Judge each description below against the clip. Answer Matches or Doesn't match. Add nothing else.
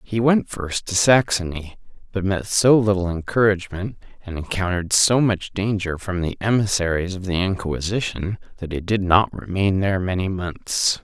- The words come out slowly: Doesn't match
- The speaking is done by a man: Matches